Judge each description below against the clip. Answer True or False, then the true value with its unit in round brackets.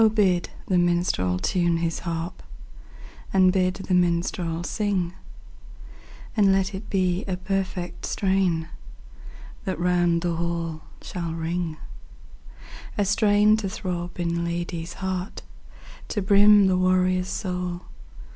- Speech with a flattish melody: True (2.0 semitones)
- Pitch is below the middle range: False (180 Hz)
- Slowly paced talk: True (120 wpm)